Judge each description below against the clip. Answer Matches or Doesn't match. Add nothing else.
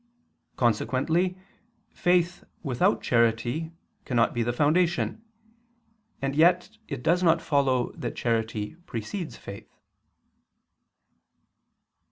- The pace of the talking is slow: Matches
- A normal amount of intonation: Doesn't match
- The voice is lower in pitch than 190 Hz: Matches